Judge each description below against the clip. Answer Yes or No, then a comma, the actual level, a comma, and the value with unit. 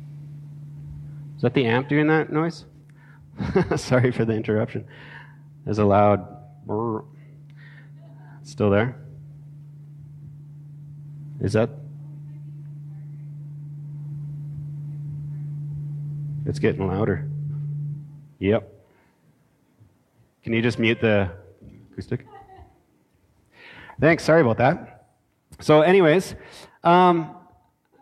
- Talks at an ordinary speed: No, slow, 75 wpm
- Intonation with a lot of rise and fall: No, average, 2.7 semitones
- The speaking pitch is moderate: Yes, medium, 145 Hz